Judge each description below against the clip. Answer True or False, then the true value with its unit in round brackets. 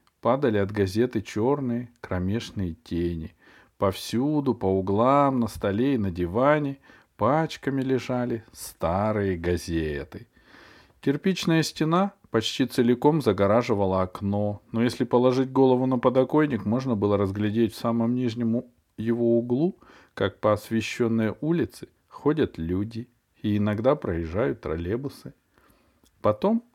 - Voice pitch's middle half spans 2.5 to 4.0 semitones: False (4.5 semitones)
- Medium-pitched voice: False (115 Hz)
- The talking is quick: False (110 wpm)